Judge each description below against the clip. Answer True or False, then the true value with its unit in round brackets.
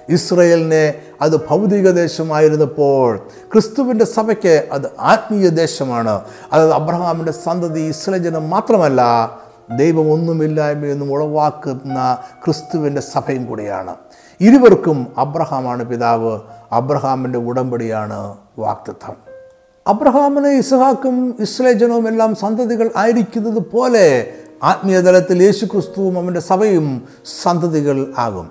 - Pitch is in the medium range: True (160 Hz)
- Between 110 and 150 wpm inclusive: False (80 wpm)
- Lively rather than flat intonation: True (7.4 semitones)